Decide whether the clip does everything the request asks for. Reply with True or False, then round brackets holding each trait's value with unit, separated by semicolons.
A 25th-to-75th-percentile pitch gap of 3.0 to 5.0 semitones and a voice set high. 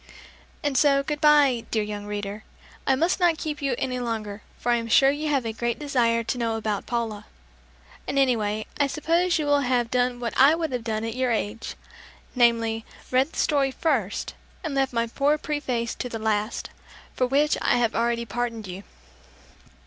True (3.8 semitones; 245 Hz)